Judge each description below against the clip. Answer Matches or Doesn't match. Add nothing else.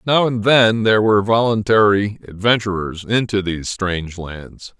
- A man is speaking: Matches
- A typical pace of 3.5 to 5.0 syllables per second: Matches